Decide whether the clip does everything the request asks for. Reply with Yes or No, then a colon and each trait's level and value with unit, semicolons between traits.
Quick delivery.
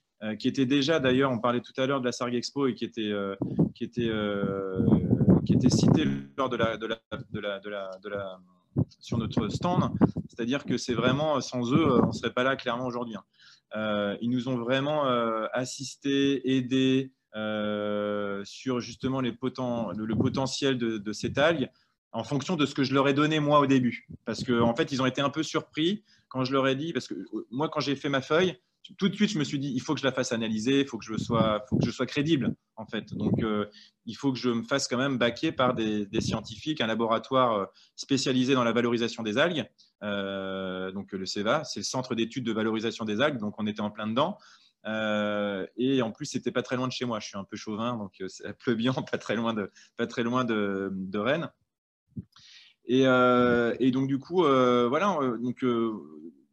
Yes: fast, 210 wpm